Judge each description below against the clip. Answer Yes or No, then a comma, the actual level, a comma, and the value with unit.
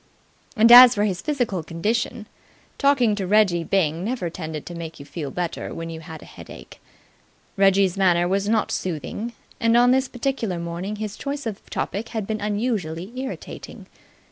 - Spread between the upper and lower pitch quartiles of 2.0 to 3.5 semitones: No, average, 5.2 semitones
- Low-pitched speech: No, high, 200 Hz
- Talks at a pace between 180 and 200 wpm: No, average, 170 wpm